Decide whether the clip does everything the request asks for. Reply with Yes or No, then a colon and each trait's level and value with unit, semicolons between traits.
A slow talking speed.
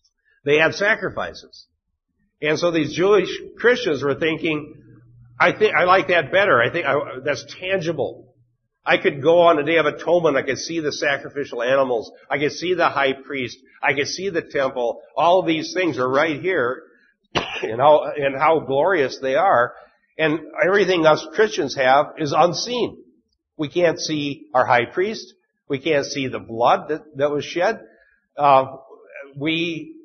No: average, 165 wpm